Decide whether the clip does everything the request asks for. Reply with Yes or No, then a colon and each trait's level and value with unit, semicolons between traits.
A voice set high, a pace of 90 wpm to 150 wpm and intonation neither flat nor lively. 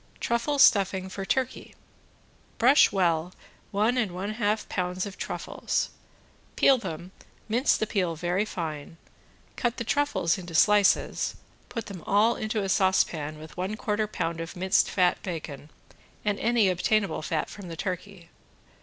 Yes: high, 195 Hz; average, 145 wpm; average, 3.7 semitones